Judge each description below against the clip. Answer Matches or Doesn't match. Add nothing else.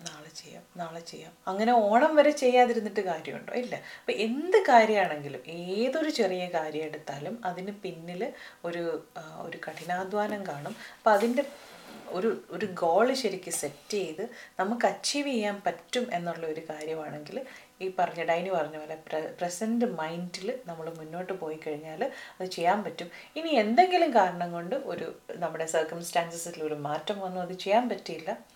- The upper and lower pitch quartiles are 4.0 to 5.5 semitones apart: Matches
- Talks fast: Matches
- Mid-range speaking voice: Matches